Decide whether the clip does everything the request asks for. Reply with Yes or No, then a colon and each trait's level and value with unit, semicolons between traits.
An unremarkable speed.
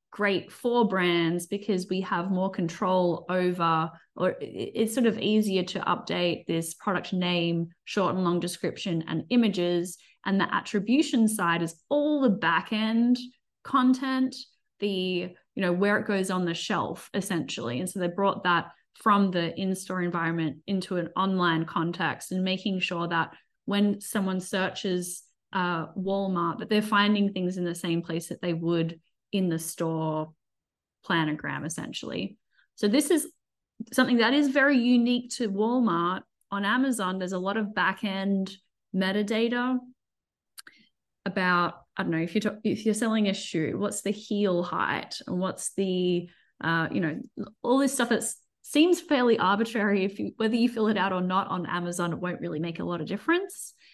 Yes: average, 165 wpm